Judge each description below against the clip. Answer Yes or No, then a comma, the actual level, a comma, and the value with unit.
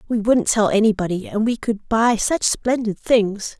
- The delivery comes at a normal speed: Yes, average, 185 wpm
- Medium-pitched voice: No, high, 220 Hz